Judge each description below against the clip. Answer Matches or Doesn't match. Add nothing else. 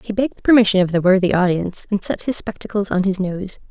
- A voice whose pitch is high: Matches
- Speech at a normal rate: Doesn't match